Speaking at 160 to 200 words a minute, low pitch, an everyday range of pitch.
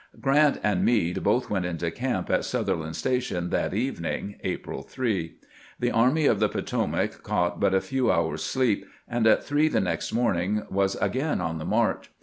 No: average, 180 wpm; low, 105 Hz; wide, 6.2 semitones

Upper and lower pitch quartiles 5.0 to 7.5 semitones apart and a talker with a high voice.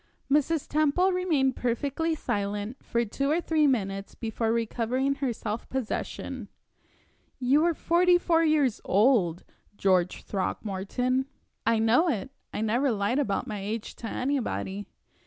Yes: wide, 5.6 semitones; very high, 250 Hz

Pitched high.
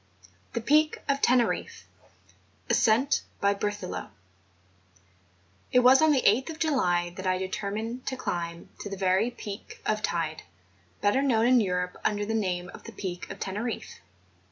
Yes: high, 210 Hz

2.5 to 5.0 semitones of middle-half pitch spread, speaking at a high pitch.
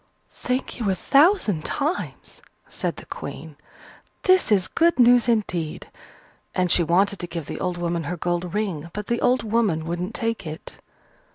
No: wide, 5.5 semitones; high, 195 Hz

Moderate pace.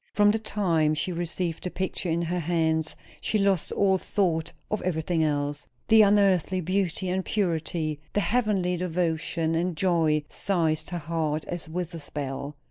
Yes: average, 160 wpm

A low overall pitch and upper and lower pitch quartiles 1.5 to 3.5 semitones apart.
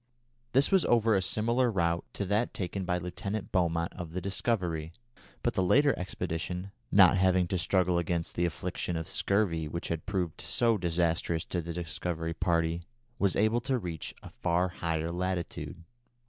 Yes: very low, 90 Hz; average, 2.9 semitones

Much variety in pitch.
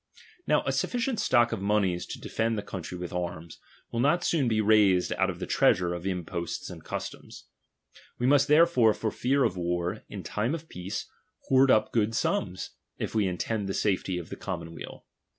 Yes: wide, 5.9 semitones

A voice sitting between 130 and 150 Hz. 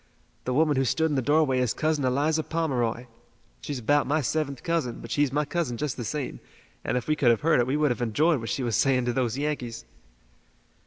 Yes: medium, 140 Hz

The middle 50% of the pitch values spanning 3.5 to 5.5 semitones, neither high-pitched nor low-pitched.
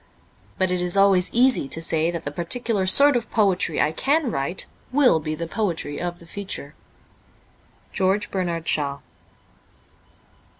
Yes: average, 4.1 semitones; medium, 180 Hz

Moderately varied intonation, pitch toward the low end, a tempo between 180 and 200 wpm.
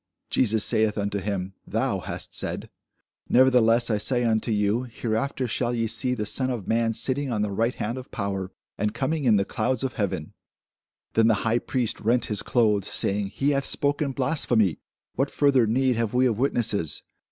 Yes: average, 3.4 semitones; low, 115 Hz; average, 185 wpm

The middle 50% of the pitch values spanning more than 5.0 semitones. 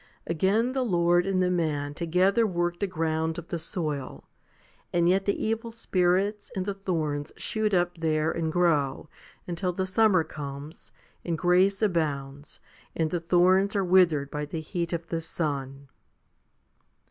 No: average, 3.1 semitones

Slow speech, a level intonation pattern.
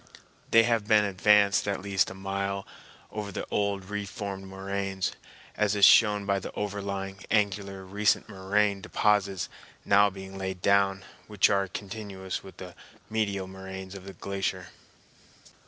No: average, 145 wpm; narrow, 1.2 semitones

